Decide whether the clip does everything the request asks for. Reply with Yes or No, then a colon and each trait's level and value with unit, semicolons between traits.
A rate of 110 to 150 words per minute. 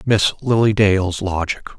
Yes: slow, 135 wpm